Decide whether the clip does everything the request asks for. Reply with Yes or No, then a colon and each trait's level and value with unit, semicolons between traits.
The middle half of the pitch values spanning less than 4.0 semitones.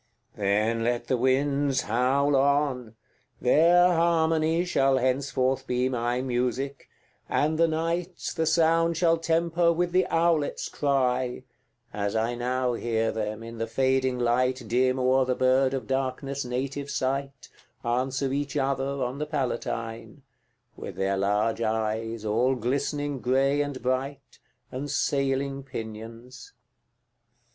Yes: average, 2.8 semitones